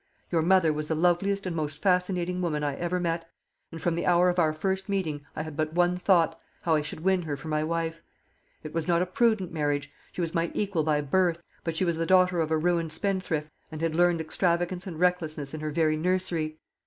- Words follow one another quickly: Yes, fast, 230 wpm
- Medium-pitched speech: Yes, medium, 165 Hz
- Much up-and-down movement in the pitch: No, narrow, 2.4 semitones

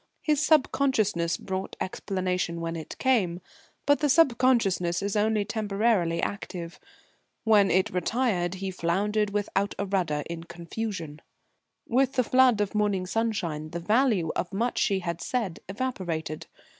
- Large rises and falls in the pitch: No, average, 4.7 semitones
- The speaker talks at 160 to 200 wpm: No, slow, 135 wpm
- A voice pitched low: No, high, 195 Hz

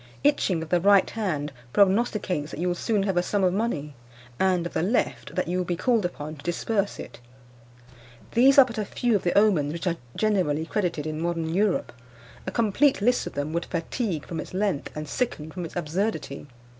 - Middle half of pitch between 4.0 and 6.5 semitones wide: Yes, average, 4.5 semitones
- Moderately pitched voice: Yes, medium, 180 Hz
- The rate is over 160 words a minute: Yes, fast, 205 wpm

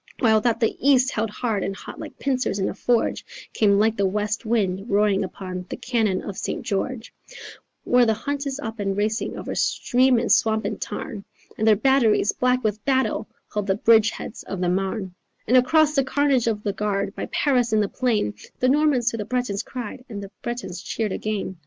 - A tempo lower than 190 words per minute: No, fast, 205 wpm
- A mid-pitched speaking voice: No, high, 220 Hz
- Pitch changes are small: No, average, 3.7 semitones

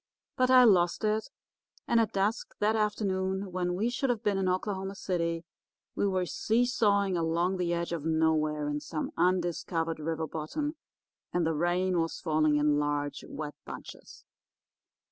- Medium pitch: Yes, medium, 180 Hz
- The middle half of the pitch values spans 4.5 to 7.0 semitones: No, average, 4.1 semitones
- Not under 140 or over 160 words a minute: Yes, average, 155 wpm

